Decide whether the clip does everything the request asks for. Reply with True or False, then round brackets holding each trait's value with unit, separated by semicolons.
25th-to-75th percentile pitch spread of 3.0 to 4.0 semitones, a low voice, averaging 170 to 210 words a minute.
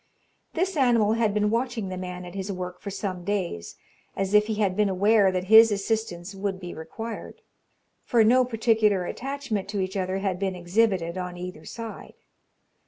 False (3.4 semitones; 200 Hz; 175 wpm)